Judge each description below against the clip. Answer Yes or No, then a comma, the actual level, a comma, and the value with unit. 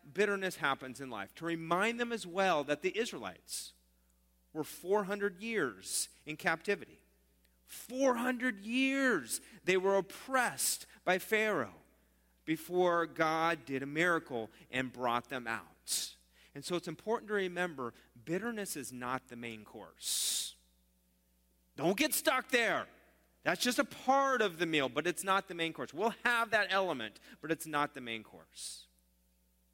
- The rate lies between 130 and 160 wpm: Yes, average, 145 wpm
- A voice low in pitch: No, medium, 165 Hz